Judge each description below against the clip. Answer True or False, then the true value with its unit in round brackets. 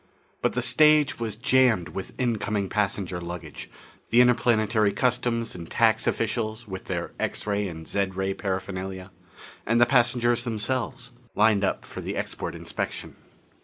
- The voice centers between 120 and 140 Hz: False (110 Hz)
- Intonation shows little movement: False (3.8 semitones)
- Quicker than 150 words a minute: False (145 wpm)